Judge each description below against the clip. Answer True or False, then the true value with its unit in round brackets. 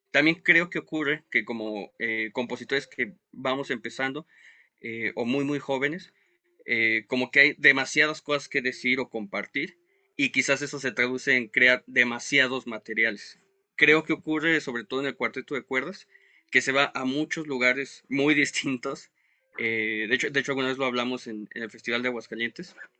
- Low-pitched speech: True (130 Hz)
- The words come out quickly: False (175 wpm)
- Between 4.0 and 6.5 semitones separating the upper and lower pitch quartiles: False (3.6 semitones)